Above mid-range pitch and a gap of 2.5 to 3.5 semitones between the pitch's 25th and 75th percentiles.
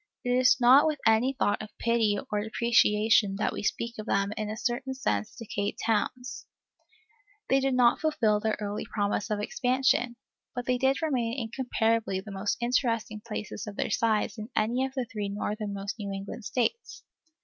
Yes: high, 225 Hz; average, 3.0 semitones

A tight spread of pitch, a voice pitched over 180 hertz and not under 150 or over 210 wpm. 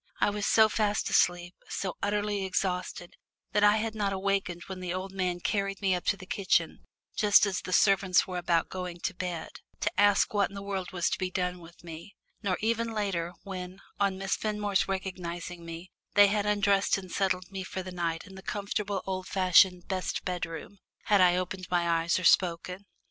Yes: narrow, 2.0 semitones; high, 190 Hz; average, 195 wpm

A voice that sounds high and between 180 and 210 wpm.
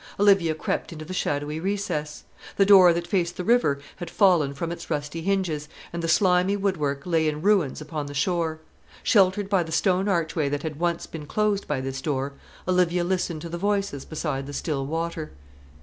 No: medium, 170 Hz; average, 190 wpm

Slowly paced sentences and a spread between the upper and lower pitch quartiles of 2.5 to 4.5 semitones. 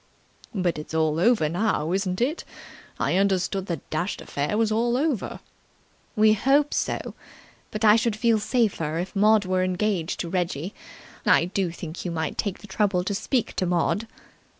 No: average, 170 wpm; average, 3.9 semitones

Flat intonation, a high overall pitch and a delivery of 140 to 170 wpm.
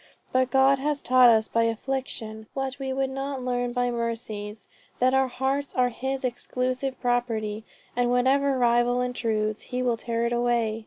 Yes: narrow, 2.3 semitones; high, 245 Hz; average, 165 wpm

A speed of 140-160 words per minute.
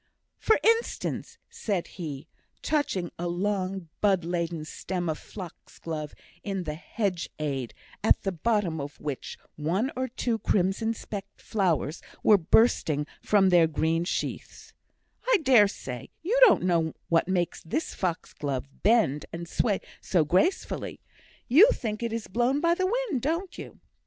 Yes: average, 150 wpm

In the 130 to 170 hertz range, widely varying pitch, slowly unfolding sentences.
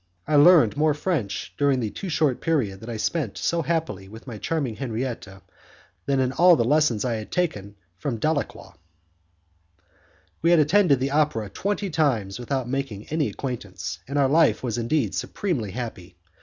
No: low, 135 Hz; wide, 5.7 semitones; average, 170 wpm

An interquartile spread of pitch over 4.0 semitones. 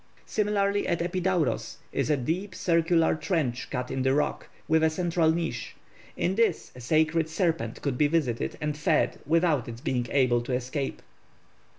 Yes: average, 4.6 semitones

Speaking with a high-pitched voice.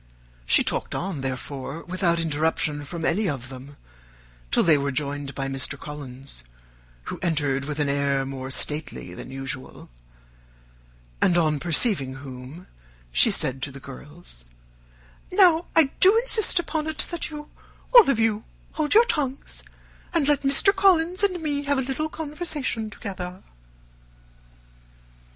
No: medium, 165 Hz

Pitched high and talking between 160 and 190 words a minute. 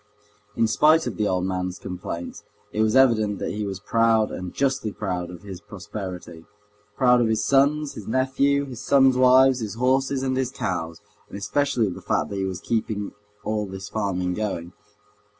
No: low, 110 Hz; average, 185 wpm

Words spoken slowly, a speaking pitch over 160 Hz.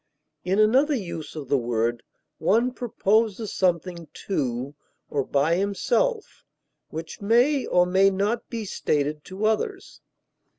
Yes: slow, 125 wpm; high, 190 Hz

